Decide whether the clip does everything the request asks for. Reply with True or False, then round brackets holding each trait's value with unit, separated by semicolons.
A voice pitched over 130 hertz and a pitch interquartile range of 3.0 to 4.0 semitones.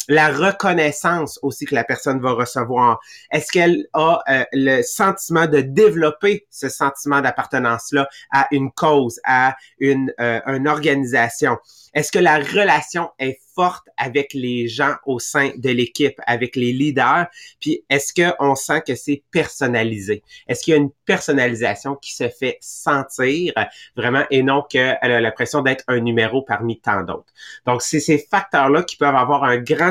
True (140 Hz; 3.4 semitones)